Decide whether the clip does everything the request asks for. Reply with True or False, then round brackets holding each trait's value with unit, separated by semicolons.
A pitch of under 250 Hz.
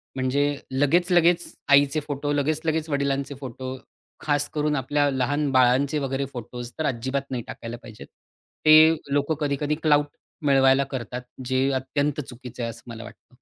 True (140 Hz)